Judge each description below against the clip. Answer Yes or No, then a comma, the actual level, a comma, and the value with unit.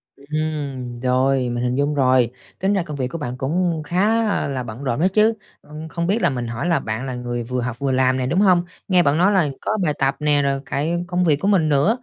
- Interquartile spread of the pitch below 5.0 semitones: No, average, 5.3 semitones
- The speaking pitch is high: No, medium, 145 Hz